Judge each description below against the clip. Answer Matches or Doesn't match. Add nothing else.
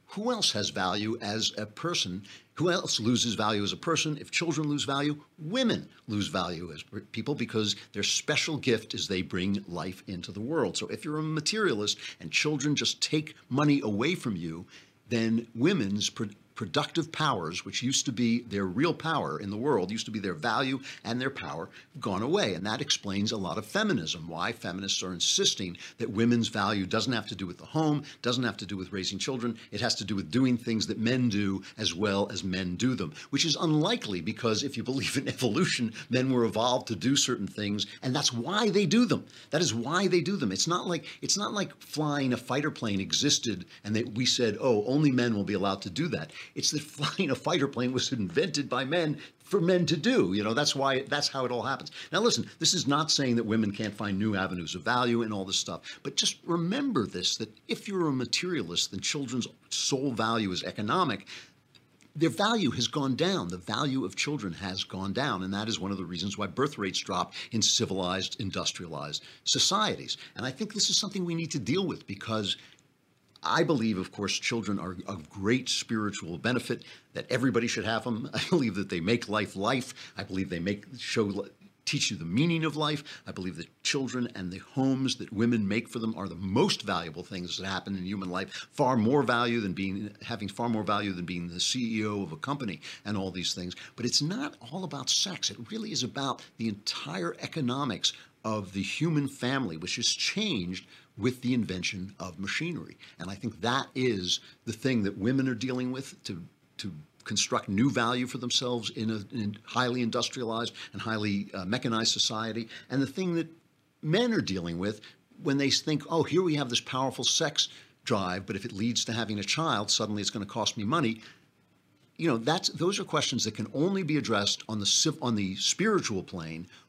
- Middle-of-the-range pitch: Doesn't match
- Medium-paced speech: Doesn't match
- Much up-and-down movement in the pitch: Matches